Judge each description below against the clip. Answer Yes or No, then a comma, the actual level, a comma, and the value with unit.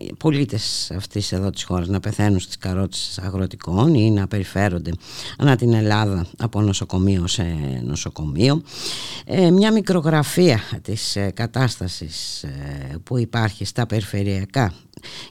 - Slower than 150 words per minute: Yes, average, 120 wpm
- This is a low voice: Yes, low, 100 Hz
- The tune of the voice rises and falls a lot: No, average, 4.3 semitones